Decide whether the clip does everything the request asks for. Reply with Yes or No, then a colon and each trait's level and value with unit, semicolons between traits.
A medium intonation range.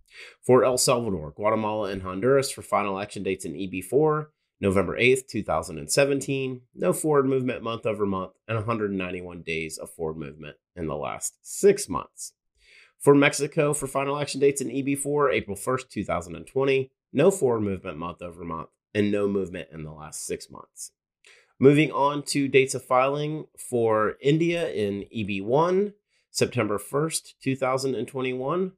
No: wide, 6.3 semitones